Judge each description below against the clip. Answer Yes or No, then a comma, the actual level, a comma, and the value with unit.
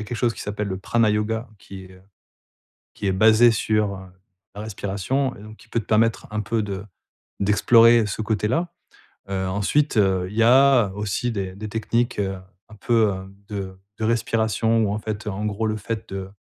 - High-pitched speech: No, low, 105 Hz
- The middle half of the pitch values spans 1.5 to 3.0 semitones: Yes, narrow, 2.4 semitones